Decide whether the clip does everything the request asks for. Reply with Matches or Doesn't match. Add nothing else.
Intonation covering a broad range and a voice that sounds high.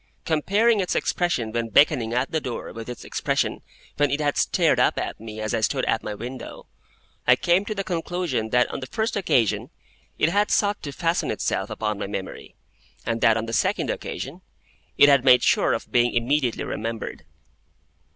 Doesn't match